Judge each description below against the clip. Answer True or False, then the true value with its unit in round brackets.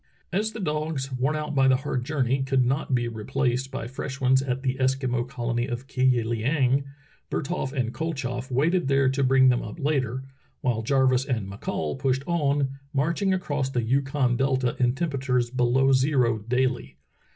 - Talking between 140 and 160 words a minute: False (175 wpm)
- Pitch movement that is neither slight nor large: False (1.8 semitones)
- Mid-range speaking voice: False (130 Hz)